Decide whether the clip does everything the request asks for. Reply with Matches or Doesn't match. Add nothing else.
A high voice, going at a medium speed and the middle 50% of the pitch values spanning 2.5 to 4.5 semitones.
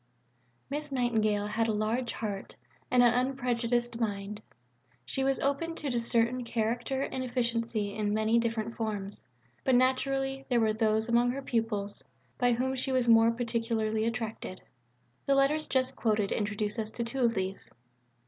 Matches